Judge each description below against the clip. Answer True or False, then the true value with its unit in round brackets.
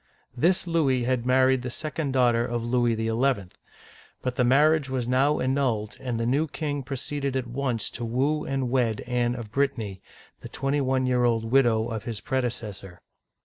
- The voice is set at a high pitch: False (125 Hz)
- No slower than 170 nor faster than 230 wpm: True (175 wpm)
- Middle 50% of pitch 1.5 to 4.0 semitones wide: True (2.6 semitones)